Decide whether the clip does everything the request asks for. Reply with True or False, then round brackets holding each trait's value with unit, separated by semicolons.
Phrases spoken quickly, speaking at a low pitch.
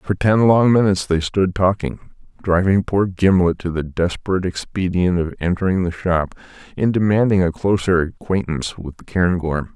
False (160 wpm; 90 Hz)